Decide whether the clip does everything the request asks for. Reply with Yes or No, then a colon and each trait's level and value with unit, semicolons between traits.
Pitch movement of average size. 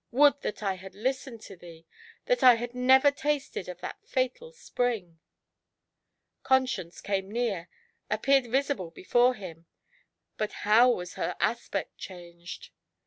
No: wide, 5.9 semitones